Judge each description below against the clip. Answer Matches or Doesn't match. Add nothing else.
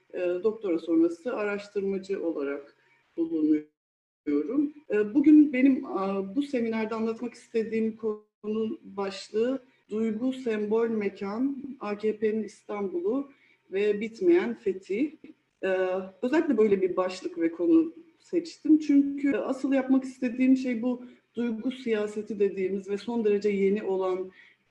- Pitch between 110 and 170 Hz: Doesn't match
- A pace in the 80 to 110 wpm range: Matches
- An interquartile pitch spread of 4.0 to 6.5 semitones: Matches